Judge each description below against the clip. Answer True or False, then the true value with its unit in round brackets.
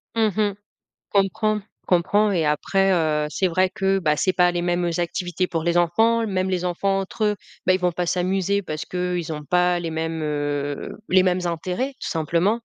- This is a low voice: False (180 Hz)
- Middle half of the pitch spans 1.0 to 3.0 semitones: True (2.6 semitones)